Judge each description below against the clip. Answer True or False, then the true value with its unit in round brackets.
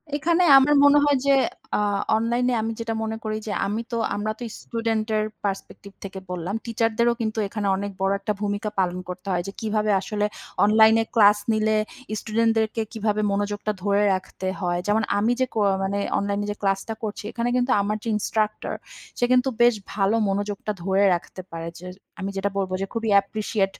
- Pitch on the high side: True (215 Hz)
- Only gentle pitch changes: True (2.1 semitones)